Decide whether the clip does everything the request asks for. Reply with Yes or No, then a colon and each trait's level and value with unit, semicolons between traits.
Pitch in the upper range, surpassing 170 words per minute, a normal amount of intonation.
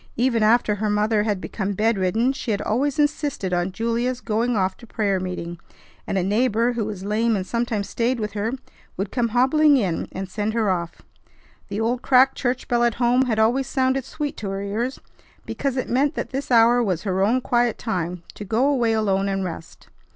Yes: high, 225 Hz; average, 200 wpm; average, 3.7 semitones